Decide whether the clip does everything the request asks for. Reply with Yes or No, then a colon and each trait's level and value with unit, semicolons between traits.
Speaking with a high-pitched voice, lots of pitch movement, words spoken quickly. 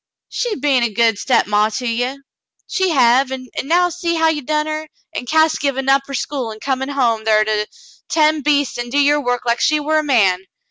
No: very high, 270 Hz; average, 4.3 semitones; fast, 215 wpm